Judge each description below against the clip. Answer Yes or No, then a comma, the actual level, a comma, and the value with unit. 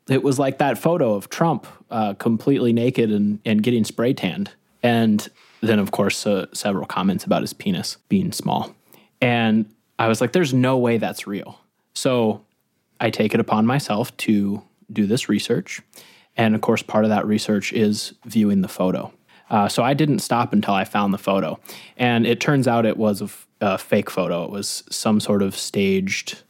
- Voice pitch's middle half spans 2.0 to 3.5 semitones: Yes, average, 3.2 semitones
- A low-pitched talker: Yes, low, 115 Hz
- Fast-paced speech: No, average, 190 wpm